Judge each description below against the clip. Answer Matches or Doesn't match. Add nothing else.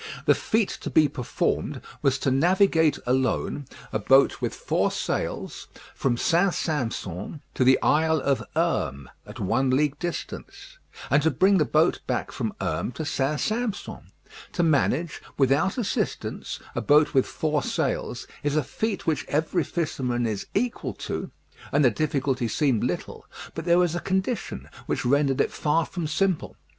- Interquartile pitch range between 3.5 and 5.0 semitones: Matches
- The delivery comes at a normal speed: Matches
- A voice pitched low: Doesn't match